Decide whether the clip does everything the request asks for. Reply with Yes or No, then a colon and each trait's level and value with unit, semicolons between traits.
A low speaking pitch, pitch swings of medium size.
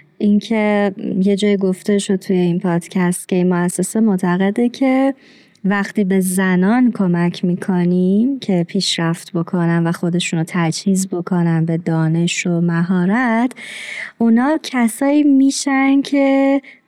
No: high, 195 Hz; average, 5.0 semitones